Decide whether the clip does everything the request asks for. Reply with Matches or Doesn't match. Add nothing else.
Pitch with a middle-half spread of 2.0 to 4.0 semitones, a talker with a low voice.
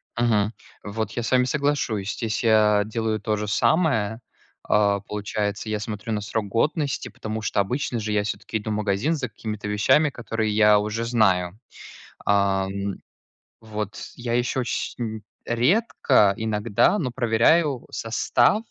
Matches